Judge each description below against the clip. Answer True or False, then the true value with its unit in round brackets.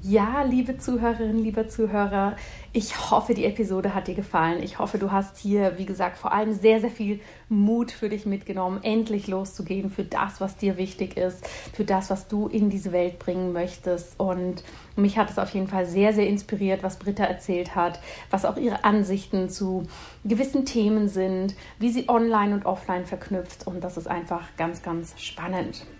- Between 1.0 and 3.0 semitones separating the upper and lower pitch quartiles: True (2.4 semitones)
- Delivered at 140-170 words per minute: False (185 wpm)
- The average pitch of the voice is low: False (195 Hz)